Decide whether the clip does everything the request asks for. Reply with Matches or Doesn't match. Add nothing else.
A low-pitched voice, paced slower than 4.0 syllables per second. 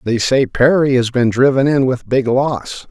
Doesn't match